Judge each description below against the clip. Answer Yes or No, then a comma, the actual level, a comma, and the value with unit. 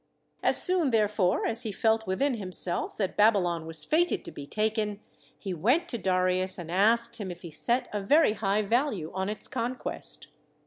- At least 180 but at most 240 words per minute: Yes, average, 185 wpm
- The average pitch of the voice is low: No, high, 210 Hz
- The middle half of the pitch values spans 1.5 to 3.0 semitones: No, average, 4.1 semitones